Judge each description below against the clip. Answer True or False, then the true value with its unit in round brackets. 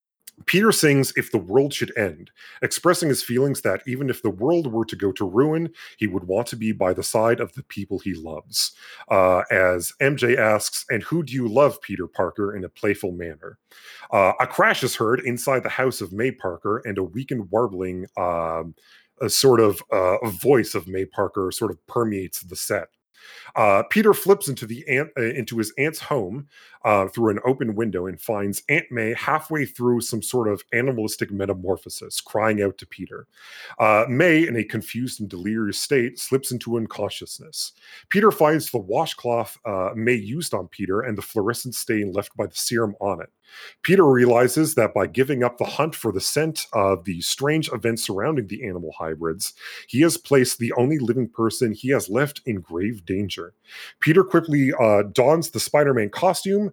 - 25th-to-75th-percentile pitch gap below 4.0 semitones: False (5.3 semitones)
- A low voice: True (120 Hz)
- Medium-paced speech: True (190 wpm)